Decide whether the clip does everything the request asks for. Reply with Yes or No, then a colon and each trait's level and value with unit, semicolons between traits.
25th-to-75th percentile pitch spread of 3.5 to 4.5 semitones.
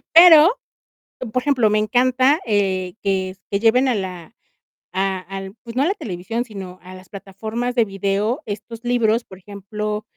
Yes: average, 4.1 semitones